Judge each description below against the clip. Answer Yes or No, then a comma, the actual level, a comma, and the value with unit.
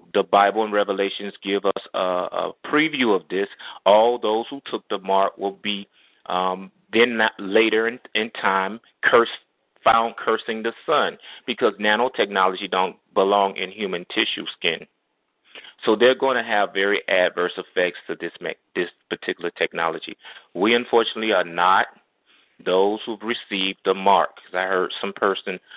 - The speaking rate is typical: Yes, average, 155 wpm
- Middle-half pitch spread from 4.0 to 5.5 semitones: No, average, 2.9 semitones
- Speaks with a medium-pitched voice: No, low, 100 Hz